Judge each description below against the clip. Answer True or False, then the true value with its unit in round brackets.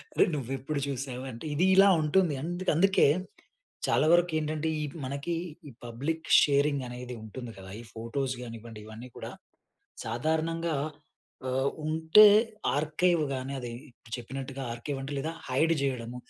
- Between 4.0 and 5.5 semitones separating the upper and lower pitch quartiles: True (4.4 semitones)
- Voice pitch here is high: False (140 Hz)